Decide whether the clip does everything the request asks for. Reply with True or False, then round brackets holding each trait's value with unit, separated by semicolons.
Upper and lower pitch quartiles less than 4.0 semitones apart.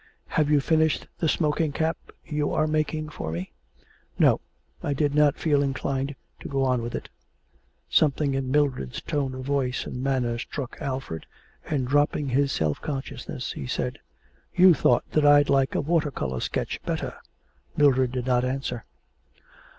True (2.6 semitones)